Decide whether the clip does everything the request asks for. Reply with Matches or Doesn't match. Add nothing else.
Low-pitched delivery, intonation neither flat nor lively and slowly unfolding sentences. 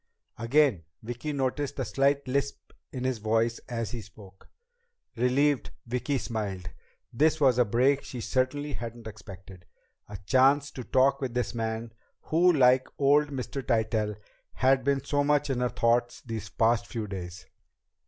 Doesn't match